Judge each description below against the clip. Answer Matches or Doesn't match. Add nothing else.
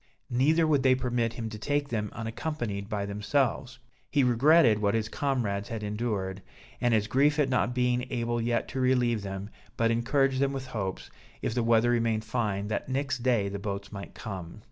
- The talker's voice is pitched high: Doesn't match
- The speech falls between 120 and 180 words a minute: Doesn't match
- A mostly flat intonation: Doesn't match